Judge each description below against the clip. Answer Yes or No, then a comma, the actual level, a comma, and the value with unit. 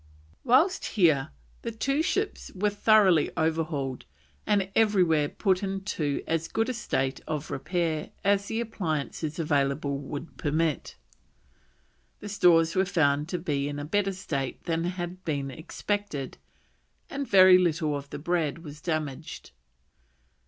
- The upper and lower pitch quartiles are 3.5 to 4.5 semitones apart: No, average, 5.0 semitones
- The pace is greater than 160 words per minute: No, slow, 135 wpm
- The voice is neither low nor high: Yes, medium, 165 Hz